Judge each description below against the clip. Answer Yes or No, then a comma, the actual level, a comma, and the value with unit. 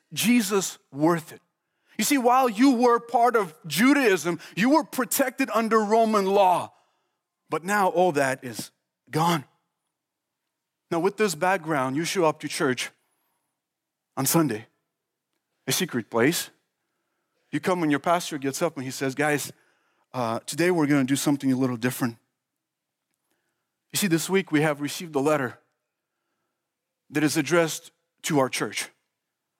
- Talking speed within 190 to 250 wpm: No, average, 150 wpm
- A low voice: No, medium, 165 Hz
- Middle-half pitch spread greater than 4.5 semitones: Yes, wide, 5.4 semitones